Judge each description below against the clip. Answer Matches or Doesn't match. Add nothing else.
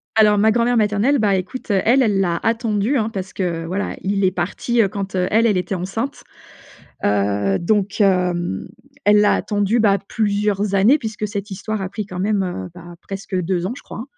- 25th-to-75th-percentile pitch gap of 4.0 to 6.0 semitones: Doesn't match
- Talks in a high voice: Matches